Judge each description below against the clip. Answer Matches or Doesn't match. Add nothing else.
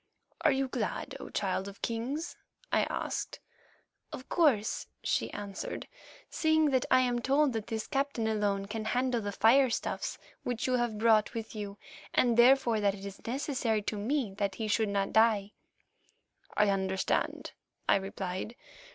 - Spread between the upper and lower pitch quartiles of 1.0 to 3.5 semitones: Doesn't match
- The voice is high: Matches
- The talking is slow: Doesn't match